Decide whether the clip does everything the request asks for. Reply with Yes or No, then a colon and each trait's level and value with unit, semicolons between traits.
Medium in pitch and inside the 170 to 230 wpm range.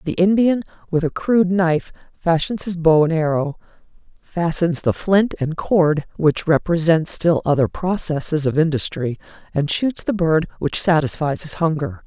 No: medium, 165 Hz; average, 155 wpm